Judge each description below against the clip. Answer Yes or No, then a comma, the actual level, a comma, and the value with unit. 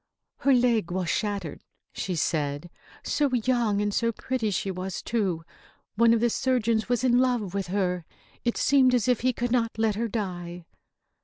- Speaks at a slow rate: No, average, 175 wpm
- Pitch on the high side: Yes, high, 220 Hz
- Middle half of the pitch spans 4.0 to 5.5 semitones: Yes, average, 4.6 semitones